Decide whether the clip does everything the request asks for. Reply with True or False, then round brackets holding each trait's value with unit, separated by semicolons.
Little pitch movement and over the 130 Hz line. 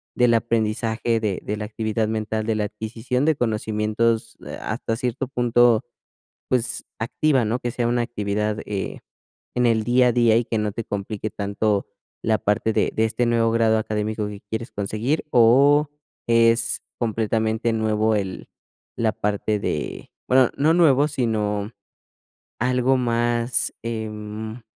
False (2.1 semitones; 115 Hz)